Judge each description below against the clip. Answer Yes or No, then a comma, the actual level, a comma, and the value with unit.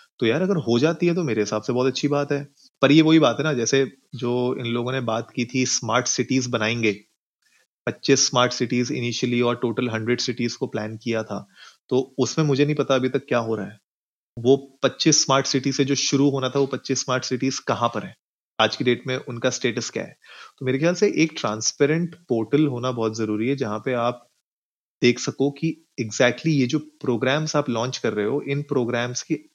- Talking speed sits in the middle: No, fast, 215 wpm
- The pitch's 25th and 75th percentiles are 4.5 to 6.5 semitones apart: No, average, 2.9 semitones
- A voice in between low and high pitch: No, low, 130 Hz